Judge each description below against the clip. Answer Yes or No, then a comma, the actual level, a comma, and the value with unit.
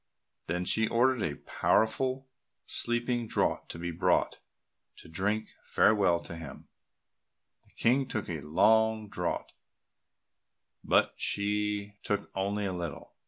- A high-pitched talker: No, low, 105 Hz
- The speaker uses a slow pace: Yes, slow, 120 wpm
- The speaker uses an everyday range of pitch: Yes, average, 4.1 semitones